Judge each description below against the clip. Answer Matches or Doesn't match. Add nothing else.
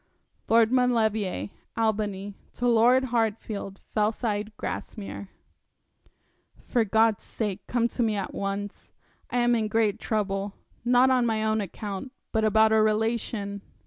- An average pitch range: Doesn't match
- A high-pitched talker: Matches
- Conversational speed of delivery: Doesn't match